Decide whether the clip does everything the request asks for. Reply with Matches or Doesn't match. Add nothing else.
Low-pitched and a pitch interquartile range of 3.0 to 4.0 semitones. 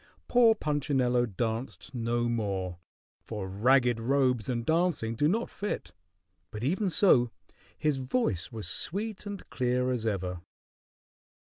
Doesn't match